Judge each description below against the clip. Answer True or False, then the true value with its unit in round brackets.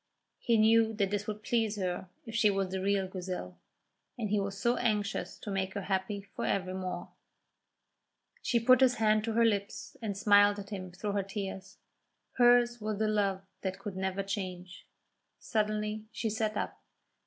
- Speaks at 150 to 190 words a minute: True (175 wpm)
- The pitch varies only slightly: True (2.2 semitones)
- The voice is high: True (205 Hz)